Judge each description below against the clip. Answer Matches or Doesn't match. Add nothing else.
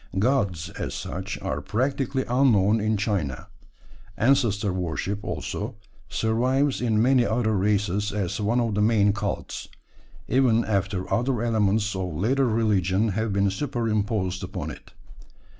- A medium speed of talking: Doesn't match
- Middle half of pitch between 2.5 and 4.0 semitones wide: Matches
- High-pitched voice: Doesn't match